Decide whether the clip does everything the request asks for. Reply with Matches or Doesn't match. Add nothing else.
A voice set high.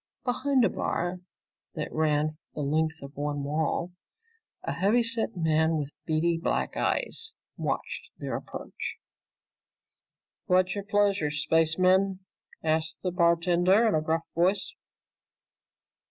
Doesn't match